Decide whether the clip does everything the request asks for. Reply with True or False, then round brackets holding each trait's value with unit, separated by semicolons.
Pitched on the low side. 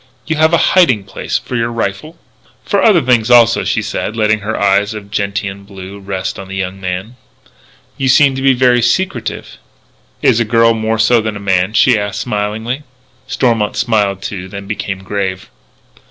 True (110 Hz)